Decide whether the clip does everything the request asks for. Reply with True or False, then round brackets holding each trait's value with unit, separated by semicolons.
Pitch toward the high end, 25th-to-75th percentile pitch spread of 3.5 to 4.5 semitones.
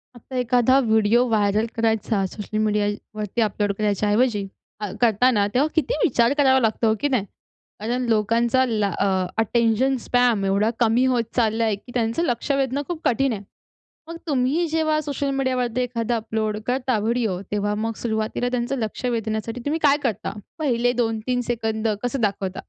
False (230 Hz; 2.9 semitones)